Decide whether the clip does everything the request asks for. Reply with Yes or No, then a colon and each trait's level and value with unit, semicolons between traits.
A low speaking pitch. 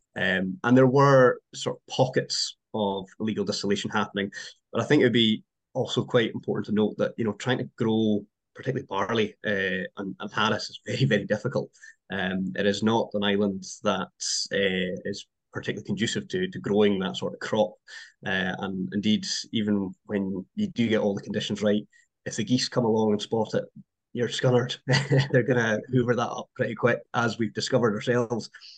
Yes: low, 110 Hz